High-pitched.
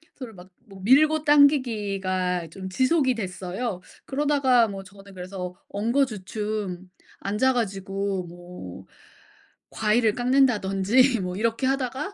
Yes: high, 210 Hz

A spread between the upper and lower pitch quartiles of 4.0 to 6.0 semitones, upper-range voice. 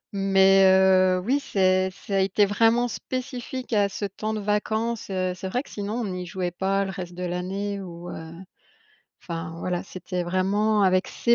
No: narrow, 2.4 semitones; high, 195 Hz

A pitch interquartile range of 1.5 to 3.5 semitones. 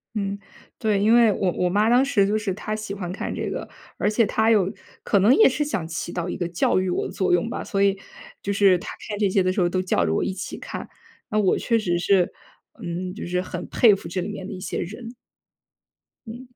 Yes: average, 3.0 semitones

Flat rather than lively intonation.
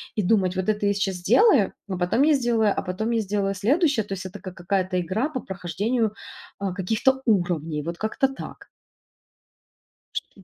No: average, 3.7 semitones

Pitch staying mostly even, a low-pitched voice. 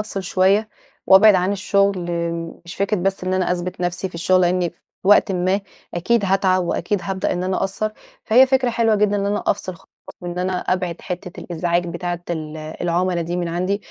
No: narrow, 2.1 semitones; medium, 185 Hz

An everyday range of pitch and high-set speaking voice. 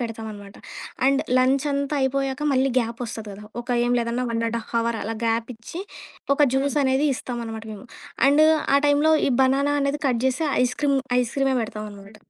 Yes: average, 3.3 semitones; very high, 250 Hz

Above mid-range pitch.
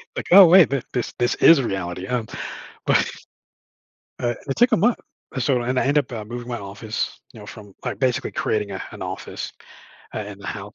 No: low, 120 Hz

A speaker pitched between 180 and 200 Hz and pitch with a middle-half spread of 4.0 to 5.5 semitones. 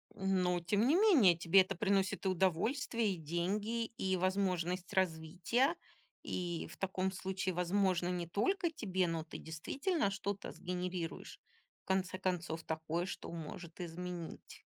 No: medium, 185 Hz; narrow, 2.6 semitones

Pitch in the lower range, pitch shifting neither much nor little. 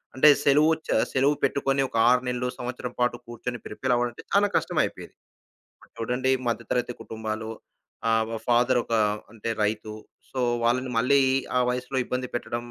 No: low, 125 Hz; narrow, 1.9 semitones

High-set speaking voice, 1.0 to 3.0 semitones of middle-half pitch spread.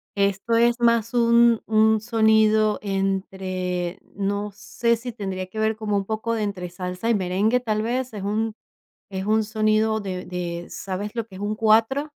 Yes: high, 215 Hz; narrow, 2.6 semitones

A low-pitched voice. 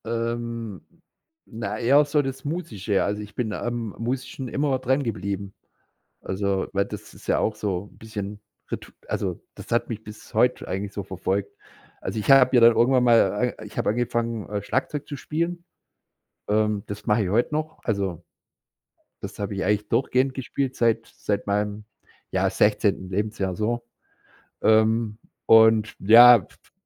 Yes: low, 110 Hz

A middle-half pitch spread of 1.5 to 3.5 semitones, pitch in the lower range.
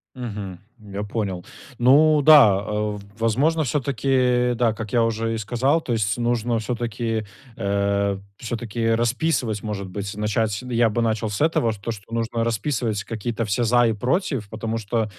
Yes: narrow, 2.5 semitones; low, 115 Hz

